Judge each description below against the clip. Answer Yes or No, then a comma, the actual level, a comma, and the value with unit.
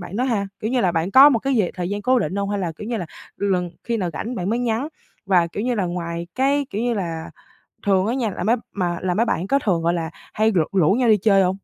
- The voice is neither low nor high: No, high, 200 Hz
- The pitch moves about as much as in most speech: Yes, average, 4.7 semitones